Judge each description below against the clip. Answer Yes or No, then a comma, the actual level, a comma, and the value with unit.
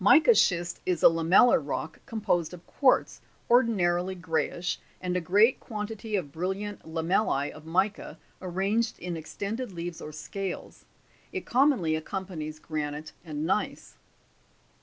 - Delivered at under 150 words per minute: Yes, average, 140 wpm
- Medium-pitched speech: Yes, medium, 180 Hz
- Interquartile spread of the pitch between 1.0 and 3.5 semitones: No, average, 4.4 semitones